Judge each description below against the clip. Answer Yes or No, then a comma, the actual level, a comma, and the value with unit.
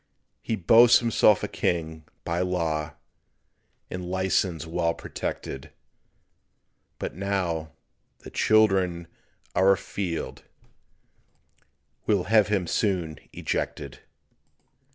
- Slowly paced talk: Yes, slow, 90 wpm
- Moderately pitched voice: No, very low, 90 Hz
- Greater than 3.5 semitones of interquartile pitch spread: No, average, 3.1 semitones